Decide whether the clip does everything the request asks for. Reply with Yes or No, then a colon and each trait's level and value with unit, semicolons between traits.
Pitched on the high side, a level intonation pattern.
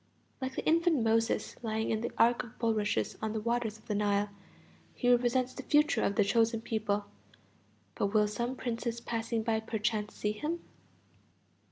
Yes: high, 225 Hz; narrow, 2.2 semitones